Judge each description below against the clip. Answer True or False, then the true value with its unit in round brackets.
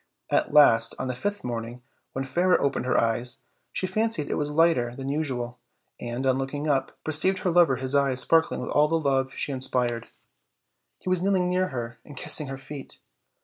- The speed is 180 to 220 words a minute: True (190 wpm)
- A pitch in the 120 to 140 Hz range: True (135 Hz)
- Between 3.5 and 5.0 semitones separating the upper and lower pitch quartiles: True (4.5 semitones)